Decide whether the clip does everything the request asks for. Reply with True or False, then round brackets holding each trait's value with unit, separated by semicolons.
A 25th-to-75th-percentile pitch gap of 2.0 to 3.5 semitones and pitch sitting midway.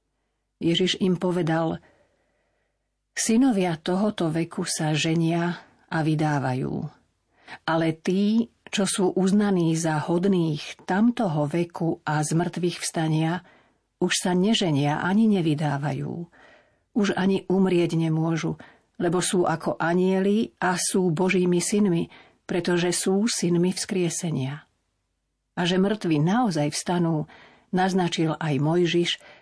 True (2.6 semitones; 175 Hz)